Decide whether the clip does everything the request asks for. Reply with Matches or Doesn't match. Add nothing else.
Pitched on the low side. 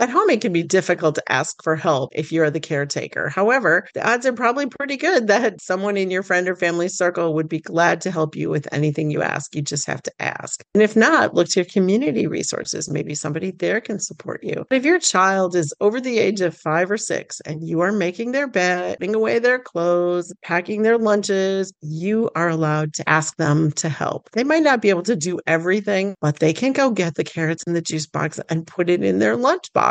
Doesn't match